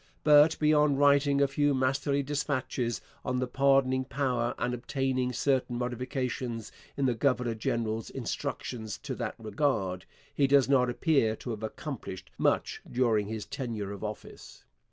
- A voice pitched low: Yes, low, 130 Hz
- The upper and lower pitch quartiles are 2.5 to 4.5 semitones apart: Yes, average, 3.3 semitones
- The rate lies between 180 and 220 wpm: No, average, 145 wpm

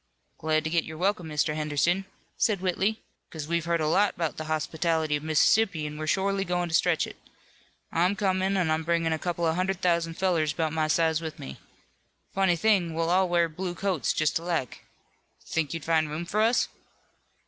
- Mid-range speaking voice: Yes, medium, 165 Hz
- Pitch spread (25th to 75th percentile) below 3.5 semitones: Yes, average, 2.8 semitones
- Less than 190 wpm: No, average, 195 wpm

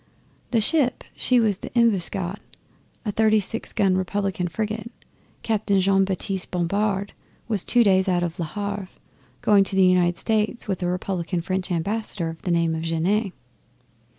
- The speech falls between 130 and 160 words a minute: Yes, average, 155 wpm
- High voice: Yes, high, 195 Hz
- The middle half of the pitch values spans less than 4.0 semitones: Yes, average, 3.0 semitones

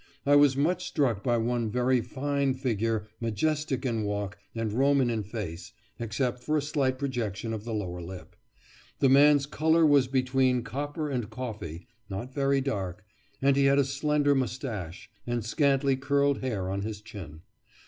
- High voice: No, low, 130 Hz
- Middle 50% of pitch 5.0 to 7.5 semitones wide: No, average, 4.6 semitones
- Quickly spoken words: No, average, 165 wpm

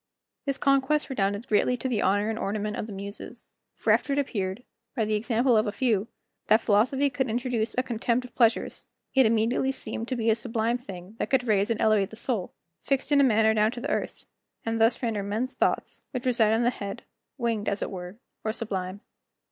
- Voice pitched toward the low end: No, high, 225 Hz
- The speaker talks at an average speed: No, fast, 210 wpm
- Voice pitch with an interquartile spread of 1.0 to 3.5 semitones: Yes, average, 3.1 semitones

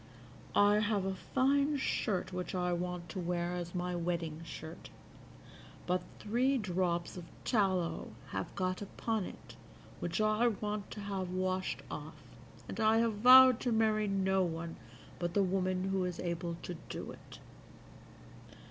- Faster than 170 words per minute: No, average, 150 wpm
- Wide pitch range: No, average, 3.2 semitones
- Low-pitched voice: No, medium, 185 Hz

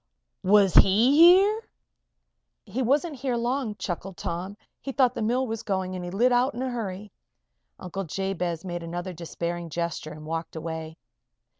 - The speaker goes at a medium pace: Yes, average, 160 wpm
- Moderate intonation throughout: No, wide, 6.1 semitones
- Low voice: No, high, 195 Hz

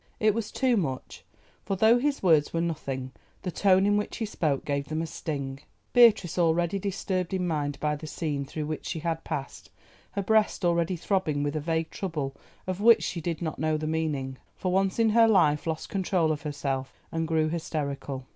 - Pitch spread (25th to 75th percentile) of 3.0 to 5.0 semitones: Yes, average, 4.3 semitones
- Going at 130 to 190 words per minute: No, average, 200 wpm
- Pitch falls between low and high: Yes, medium, 165 Hz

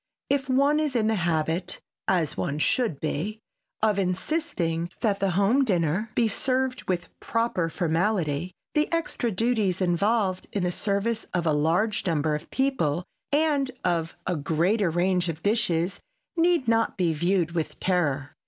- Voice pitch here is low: No, medium, 185 Hz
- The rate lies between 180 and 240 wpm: No, average, 155 wpm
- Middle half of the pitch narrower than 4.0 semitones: No, wide, 5.5 semitones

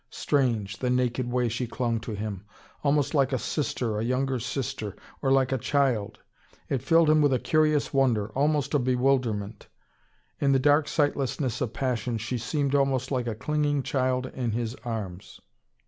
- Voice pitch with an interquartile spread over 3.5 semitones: No, average, 3.2 semitones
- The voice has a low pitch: Yes, low, 130 Hz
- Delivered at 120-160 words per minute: No, average, 170 wpm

